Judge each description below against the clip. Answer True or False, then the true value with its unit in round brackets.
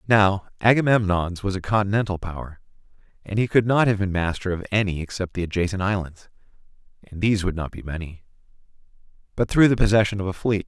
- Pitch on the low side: True (100 Hz)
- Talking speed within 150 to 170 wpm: False (180 wpm)